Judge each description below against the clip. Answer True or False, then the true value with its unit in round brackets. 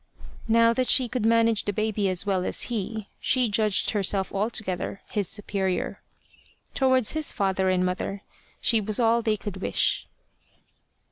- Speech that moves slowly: False (150 wpm)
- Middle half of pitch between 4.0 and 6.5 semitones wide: False (2.9 semitones)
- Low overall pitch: False (210 Hz)